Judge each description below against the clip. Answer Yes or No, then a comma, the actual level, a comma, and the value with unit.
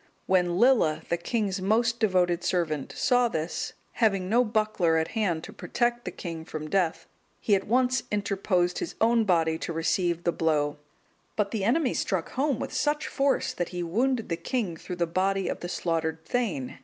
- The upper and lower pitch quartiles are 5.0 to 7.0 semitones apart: Yes, wide, 5.5 semitones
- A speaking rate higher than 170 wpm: Yes, average, 180 wpm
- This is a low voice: No, medium, 185 Hz